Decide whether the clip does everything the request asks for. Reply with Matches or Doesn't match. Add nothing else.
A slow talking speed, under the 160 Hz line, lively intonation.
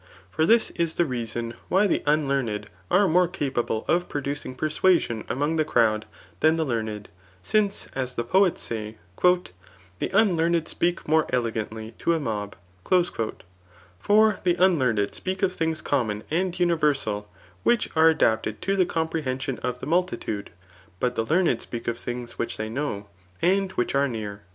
Doesn't match